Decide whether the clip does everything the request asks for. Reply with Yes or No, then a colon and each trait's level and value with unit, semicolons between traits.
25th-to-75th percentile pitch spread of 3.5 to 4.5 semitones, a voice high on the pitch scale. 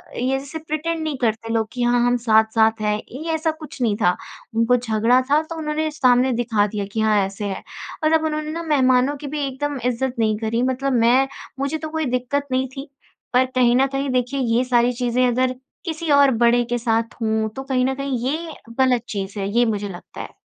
Yes: average, 3.8 semitones; very high, 255 Hz